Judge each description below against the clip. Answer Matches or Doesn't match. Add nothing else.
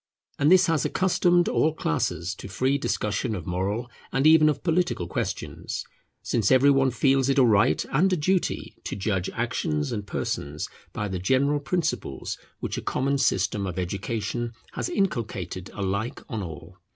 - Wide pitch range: Matches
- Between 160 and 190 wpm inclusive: Matches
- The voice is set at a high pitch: Doesn't match